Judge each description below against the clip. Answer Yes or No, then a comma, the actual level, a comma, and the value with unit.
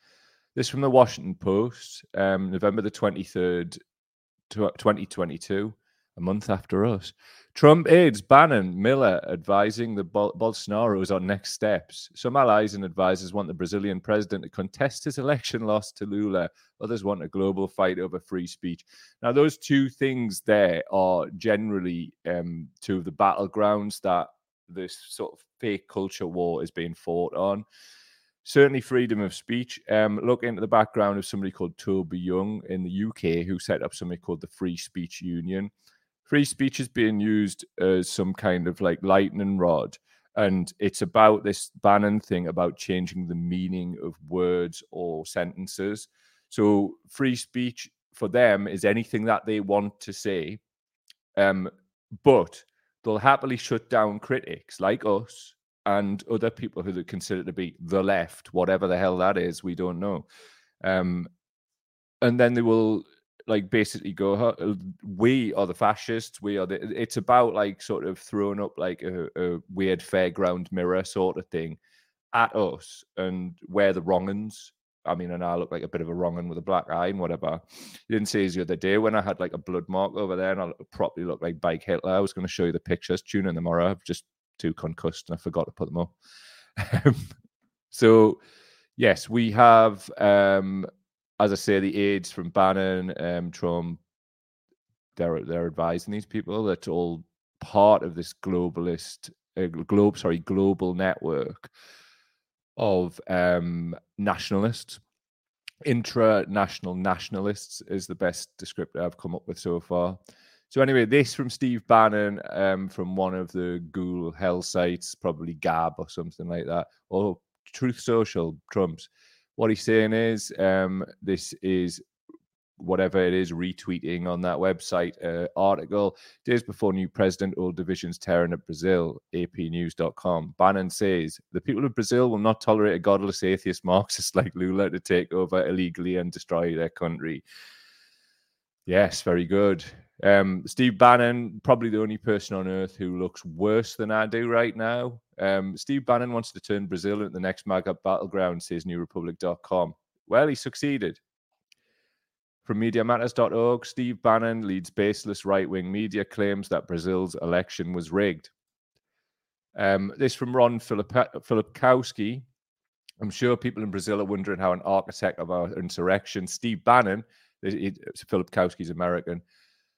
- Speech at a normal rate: Yes, average, 160 wpm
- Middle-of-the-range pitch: No, very low, 95 Hz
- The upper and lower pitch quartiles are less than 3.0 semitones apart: No, average, 3.3 semitones